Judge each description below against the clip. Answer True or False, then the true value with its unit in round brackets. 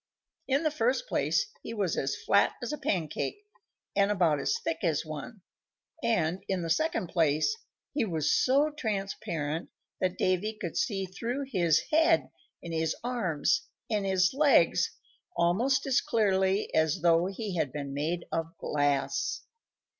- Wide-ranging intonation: True (6.2 semitones)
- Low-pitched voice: False (190 Hz)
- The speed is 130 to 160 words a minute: True (150 wpm)